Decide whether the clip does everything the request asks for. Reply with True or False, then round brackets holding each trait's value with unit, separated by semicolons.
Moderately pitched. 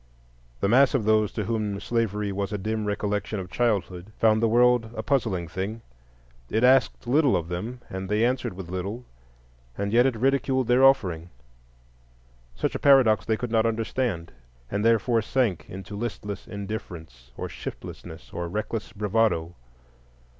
False (110 Hz)